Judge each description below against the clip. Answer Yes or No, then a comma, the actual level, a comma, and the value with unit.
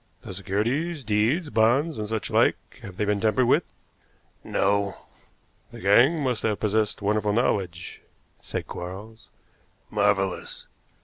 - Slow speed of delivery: Yes, slow, 125 wpm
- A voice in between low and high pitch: No, low, 105 Hz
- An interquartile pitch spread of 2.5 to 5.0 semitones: Yes, average, 2.9 semitones